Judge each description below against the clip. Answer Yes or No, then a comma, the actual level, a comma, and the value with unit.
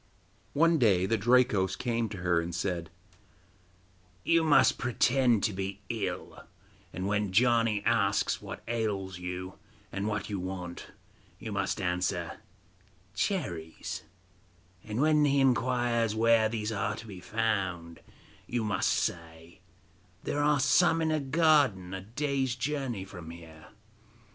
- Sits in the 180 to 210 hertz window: No, low, 110 Hz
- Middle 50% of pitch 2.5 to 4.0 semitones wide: No, wide, 5.4 semitones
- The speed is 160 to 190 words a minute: No, slow, 135 wpm